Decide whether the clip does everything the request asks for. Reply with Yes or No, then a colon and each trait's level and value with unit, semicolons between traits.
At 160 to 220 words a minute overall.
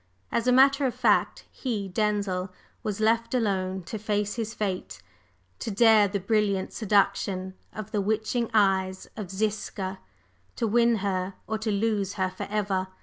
No: average, 150 wpm